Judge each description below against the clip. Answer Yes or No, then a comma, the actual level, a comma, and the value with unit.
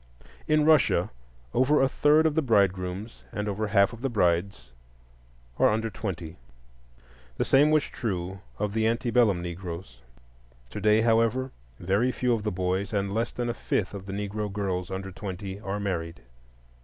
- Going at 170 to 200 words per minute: No, average, 155 wpm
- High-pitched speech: No, low, 105 Hz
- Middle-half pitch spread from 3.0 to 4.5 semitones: Yes, average, 3.8 semitones